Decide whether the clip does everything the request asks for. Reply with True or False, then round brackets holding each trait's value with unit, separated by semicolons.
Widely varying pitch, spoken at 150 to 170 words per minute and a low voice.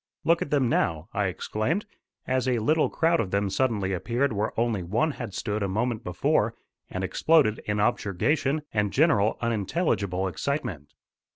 True (6.0 semitones; 160 wpm; 110 Hz)